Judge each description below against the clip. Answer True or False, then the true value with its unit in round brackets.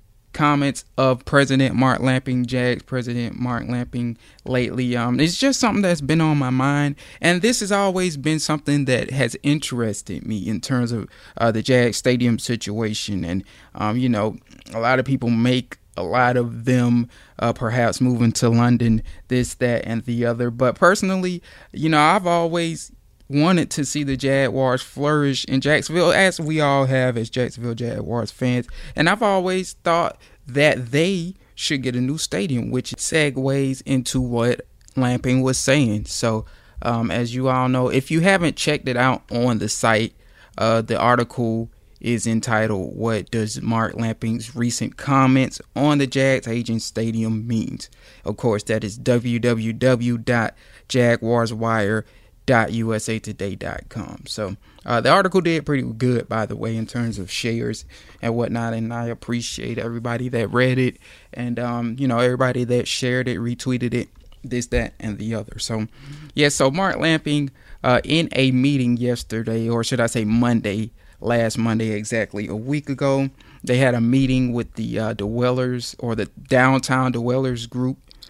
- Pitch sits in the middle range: False (120 Hz)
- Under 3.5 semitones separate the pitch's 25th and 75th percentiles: True (2.8 semitones)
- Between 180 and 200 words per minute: False (165 wpm)